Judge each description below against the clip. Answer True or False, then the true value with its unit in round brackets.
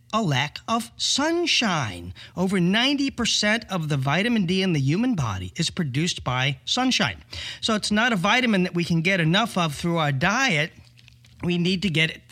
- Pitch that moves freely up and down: True (7.1 semitones)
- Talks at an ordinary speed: True (180 wpm)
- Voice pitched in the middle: True (175 Hz)